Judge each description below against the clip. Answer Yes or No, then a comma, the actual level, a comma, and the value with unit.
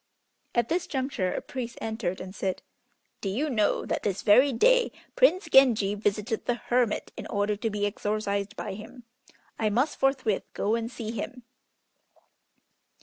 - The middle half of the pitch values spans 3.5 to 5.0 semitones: Yes, average, 3.8 semitones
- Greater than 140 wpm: Yes, average, 155 wpm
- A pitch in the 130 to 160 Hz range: No, high, 225 Hz